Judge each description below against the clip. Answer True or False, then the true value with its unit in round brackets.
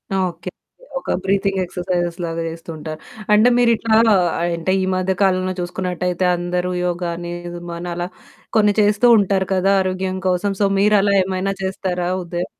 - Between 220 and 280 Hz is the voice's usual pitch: False (185 Hz)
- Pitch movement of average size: False (2.0 semitones)